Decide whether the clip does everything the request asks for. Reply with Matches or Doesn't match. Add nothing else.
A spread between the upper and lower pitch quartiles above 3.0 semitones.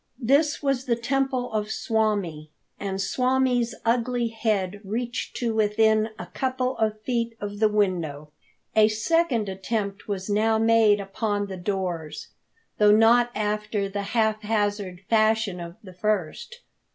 Doesn't match